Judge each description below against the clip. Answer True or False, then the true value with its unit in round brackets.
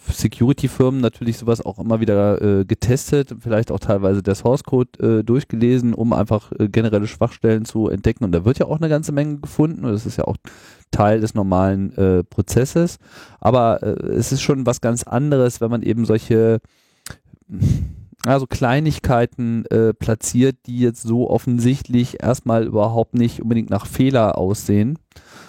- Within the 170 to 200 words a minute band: False (160 wpm)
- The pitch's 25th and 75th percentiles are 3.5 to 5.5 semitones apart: False (2.9 semitones)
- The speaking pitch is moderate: False (115 Hz)